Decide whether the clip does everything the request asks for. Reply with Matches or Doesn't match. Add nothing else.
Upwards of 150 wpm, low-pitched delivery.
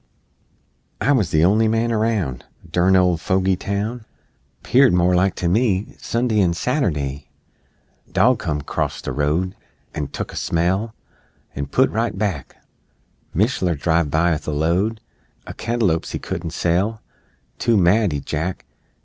Doesn't match